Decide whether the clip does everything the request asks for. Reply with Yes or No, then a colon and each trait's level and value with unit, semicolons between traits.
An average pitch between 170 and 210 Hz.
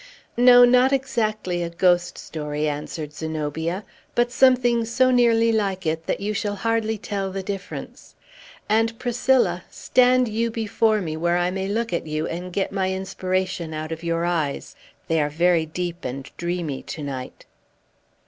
Yes: high, 190 Hz